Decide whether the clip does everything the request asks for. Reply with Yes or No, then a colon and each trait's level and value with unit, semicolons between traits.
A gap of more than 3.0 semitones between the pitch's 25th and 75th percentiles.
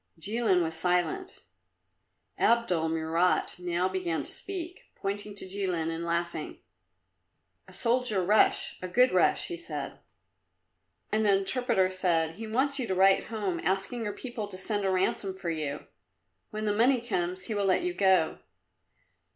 Yes: average, 4.2 semitones